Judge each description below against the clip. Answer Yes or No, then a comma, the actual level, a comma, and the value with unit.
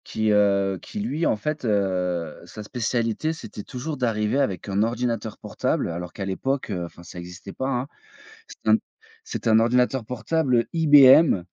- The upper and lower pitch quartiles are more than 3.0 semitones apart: Yes, average, 5.1 semitones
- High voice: No, low, 110 Hz